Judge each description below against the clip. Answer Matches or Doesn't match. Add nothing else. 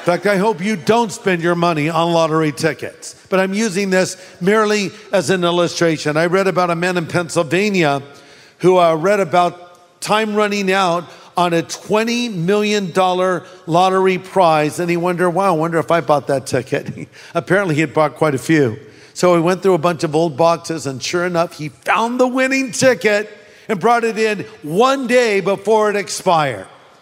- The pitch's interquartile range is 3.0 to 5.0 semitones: Matches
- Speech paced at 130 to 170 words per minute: Doesn't match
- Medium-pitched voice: Matches